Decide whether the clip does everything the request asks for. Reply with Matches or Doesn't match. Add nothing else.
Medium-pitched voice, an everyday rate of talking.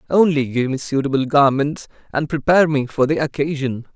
Matches